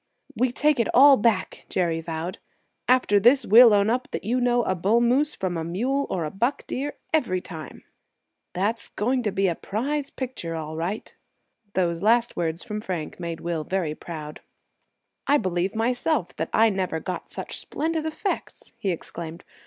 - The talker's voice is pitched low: No, high, 205 Hz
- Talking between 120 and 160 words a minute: No, average, 175 wpm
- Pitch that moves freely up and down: Yes, wide, 6.5 semitones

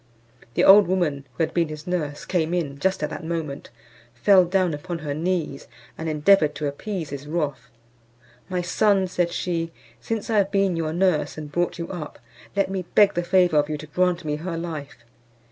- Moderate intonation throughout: Yes, average, 3.6 semitones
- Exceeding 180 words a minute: Yes, average, 195 wpm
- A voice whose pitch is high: No, medium, 170 Hz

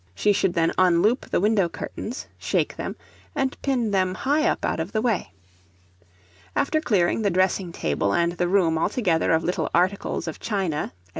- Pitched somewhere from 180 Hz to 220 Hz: Yes, medium, 185 Hz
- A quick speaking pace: No, average, 175 wpm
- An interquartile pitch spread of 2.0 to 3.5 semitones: No, average, 4.3 semitones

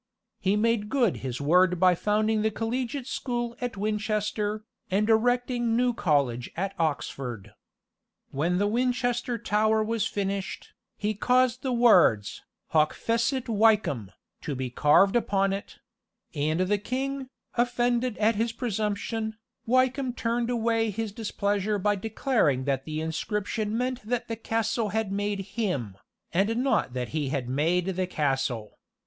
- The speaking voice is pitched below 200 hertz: No, high, 210 Hz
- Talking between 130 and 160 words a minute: Yes, average, 140 wpm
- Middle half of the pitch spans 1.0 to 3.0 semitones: No, average, 4.6 semitones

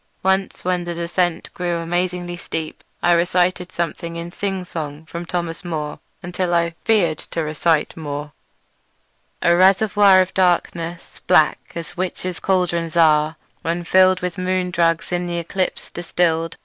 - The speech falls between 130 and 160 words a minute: Yes, average, 145 wpm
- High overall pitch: No, medium, 175 Hz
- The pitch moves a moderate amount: No, narrow, 1.5 semitones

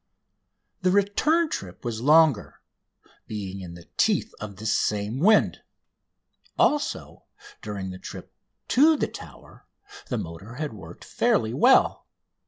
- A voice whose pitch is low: Yes, low, 115 Hz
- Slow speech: Yes, slow, 125 wpm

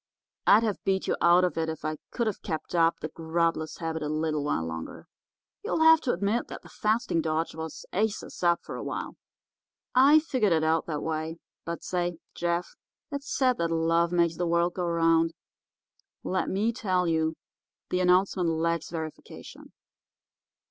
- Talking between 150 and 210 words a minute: Yes, average, 170 wpm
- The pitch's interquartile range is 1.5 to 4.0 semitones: Yes, average, 2.8 semitones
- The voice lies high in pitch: No, medium, 170 Hz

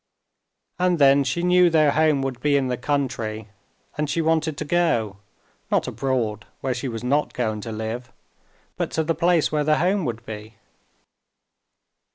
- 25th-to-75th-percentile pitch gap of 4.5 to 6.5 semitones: Yes, average, 5.2 semitones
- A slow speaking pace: No, average, 170 wpm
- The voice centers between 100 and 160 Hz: Yes, medium, 140 Hz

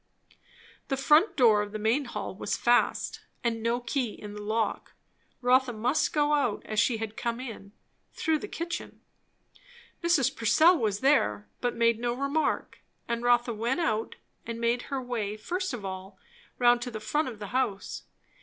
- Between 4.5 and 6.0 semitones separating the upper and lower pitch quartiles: No, average, 3.8 semitones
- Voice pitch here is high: Yes, high, 240 Hz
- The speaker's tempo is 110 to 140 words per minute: No, average, 175 wpm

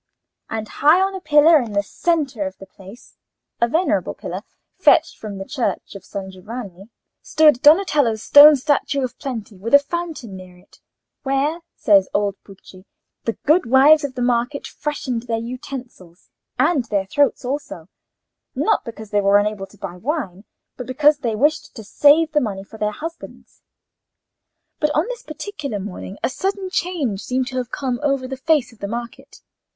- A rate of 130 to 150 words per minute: No, average, 170 wpm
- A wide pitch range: Yes, wide, 6.3 semitones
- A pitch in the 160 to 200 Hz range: No, very high, 250 Hz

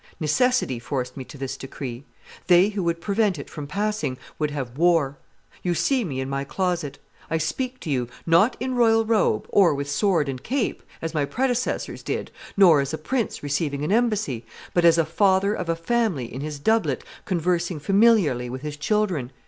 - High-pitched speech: No, medium, 165 Hz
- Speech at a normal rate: Yes, average, 190 wpm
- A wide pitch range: Yes, wide, 6.8 semitones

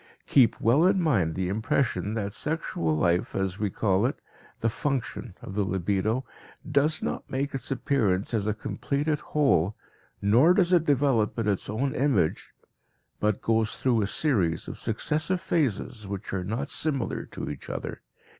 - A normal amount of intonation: No, wide, 6.0 semitones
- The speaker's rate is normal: Yes, average, 165 wpm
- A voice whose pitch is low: Yes, low, 115 Hz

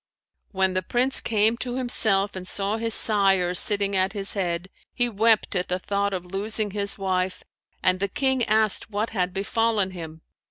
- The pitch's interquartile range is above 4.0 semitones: No, average, 2.8 semitones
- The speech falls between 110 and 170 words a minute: No, average, 185 wpm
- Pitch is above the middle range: Yes, high, 200 Hz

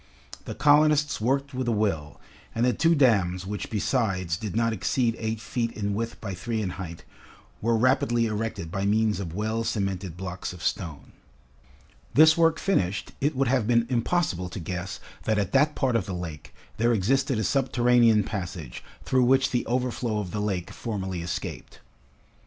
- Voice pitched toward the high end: No, low, 110 Hz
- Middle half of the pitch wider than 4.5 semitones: Yes, average, 4.9 semitones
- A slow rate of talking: No, average, 175 wpm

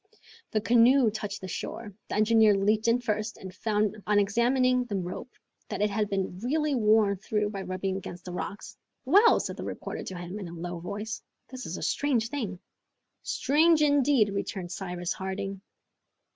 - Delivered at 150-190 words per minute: Yes, average, 175 wpm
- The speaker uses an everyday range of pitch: Yes, average, 3.7 semitones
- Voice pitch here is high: Yes, high, 210 Hz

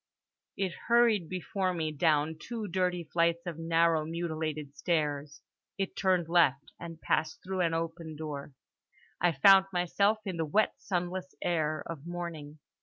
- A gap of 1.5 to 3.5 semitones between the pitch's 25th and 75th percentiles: Yes, average, 2.8 semitones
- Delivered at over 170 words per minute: No, average, 145 wpm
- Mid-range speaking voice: Yes, medium, 170 Hz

